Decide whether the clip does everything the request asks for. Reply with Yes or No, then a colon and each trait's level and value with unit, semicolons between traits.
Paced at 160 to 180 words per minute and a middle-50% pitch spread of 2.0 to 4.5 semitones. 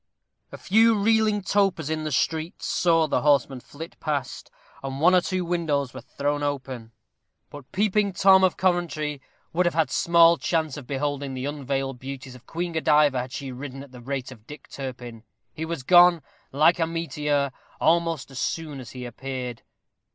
Yes: average, 175 wpm; average, 4.1 semitones